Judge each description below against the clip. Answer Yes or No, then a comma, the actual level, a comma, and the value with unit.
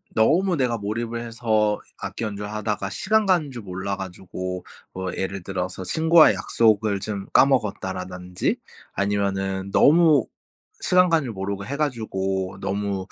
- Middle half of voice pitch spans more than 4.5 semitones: No, average, 4.0 semitones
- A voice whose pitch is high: No, low, 105 Hz